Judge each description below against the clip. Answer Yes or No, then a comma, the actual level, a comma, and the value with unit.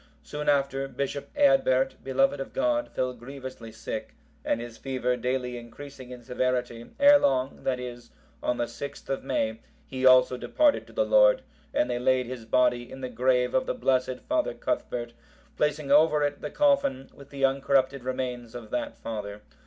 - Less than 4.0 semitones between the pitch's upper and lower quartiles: Yes, narrow, 2.5 semitones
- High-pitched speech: No, low, 130 Hz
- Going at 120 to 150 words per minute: No, average, 175 wpm